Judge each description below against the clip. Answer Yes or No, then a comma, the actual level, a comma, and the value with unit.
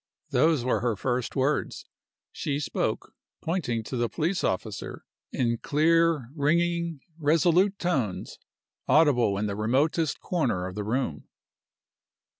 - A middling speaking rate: No, slow, 120 wpm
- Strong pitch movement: Yes, wide, 6.1 semitones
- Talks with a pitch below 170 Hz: Yes, medium, 140 Hz